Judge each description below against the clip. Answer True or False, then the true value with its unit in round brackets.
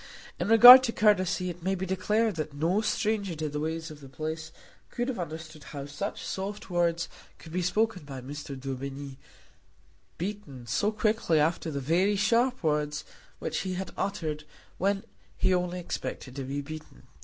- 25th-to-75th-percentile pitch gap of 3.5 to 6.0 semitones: True (5.2 semitones)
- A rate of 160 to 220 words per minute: True (170 wpm)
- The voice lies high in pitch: False (170 Hz)